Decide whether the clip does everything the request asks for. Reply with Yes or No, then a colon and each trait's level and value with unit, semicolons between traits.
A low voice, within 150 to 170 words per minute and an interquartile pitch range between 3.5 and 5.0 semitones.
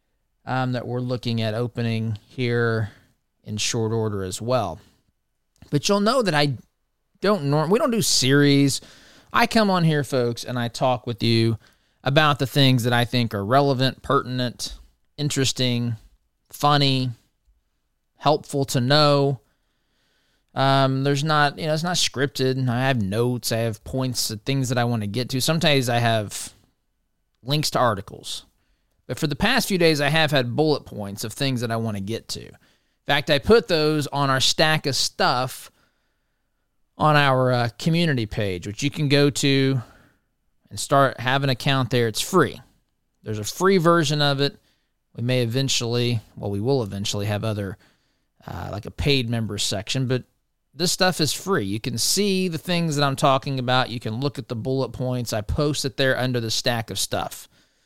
No: low, 130 Hz; average, 180 wpm; average, 3.9 semitones